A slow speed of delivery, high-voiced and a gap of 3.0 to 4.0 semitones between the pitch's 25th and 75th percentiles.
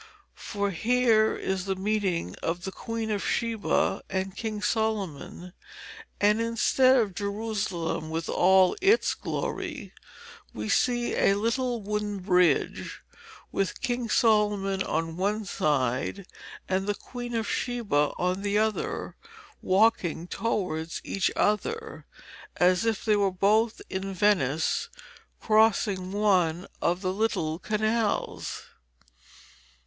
Yes: slow, 115 wpm; high, 205 Hz; average, 3.3 semitones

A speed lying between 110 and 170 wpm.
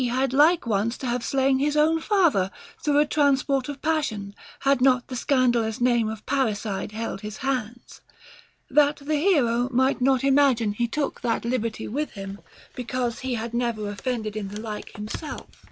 No: average, 185 wpm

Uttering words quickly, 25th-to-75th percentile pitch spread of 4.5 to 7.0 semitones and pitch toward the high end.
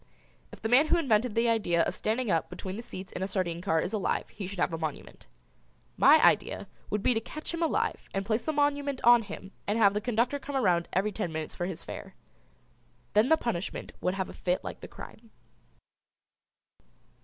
Yes: fast, 210 wpm; average, 4.8 semitones; high, 210 Hz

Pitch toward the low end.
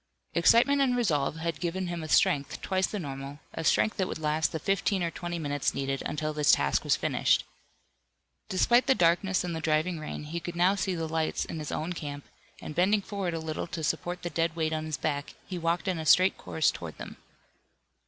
No: medium, 165 Hz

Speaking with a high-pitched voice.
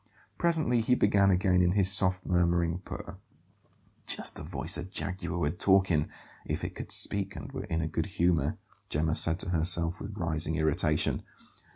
No: very low, 90 Hz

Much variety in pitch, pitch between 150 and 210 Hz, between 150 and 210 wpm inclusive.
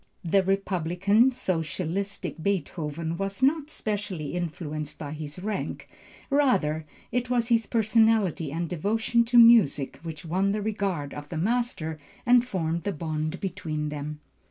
No: wide, 5.9 semitones; medium, 185 Hz; slow, 135 wpm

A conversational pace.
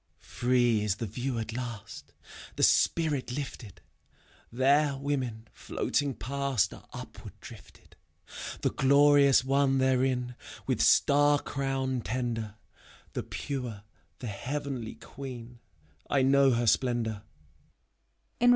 No: slow, 110 wpm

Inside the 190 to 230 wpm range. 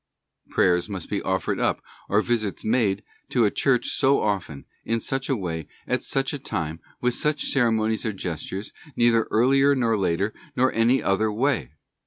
No: average, 175 wpm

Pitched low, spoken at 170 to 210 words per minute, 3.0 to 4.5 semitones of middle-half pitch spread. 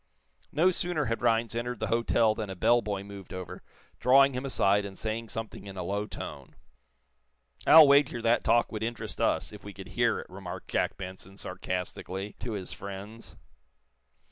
Yes: low, 110 Hz; average, 175 wpm; average, 3.3 semitones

